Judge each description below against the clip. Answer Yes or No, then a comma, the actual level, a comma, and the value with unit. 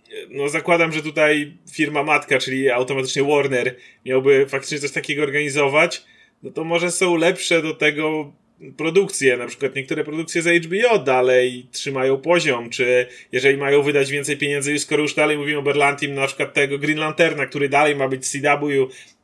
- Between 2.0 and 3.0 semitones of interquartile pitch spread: Yes, narrow, 2.4 semitones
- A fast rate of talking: Yes, fast, 170 wpm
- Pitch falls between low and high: Yes, medium, 145 Hz